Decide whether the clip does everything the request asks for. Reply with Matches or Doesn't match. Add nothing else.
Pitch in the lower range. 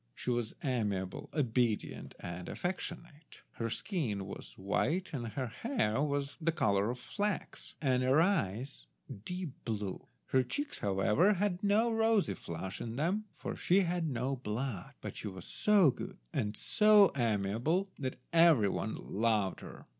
Matches